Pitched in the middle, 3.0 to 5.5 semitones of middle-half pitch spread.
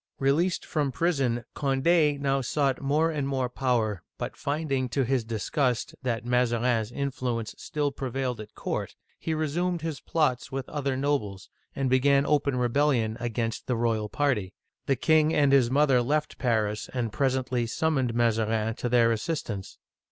No: low, 130 Hz; average, 3.5 semitones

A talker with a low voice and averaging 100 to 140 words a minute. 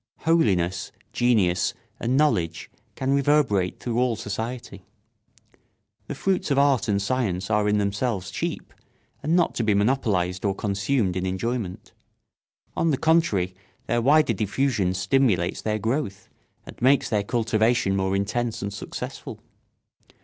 Yes: low, 110 Hz; slow, 135 wpm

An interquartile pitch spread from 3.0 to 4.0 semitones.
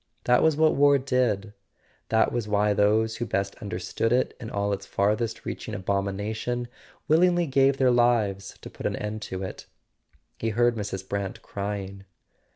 Yes: average, 3.5 semitones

